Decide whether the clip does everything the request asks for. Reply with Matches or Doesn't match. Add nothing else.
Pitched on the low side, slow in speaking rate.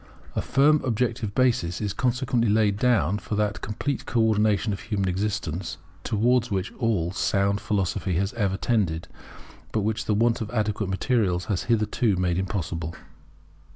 Doesn't match